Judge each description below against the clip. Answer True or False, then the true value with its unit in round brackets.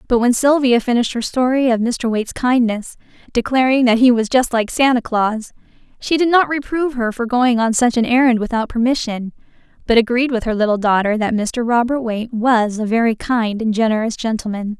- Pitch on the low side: False (235 Hz)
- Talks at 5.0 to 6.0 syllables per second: True (5.5 syllables/s)